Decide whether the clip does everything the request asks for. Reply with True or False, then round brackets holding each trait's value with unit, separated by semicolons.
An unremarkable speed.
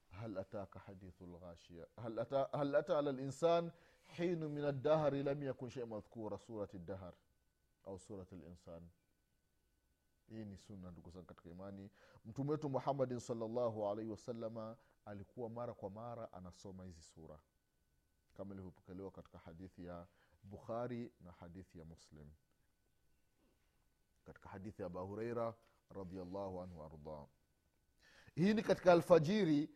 False (95 wpm)